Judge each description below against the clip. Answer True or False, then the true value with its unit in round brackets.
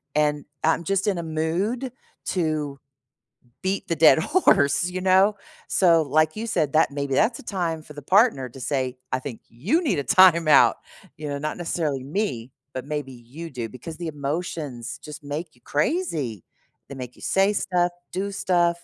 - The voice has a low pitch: False (155 Hz)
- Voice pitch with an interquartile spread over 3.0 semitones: True (4.6 semitones)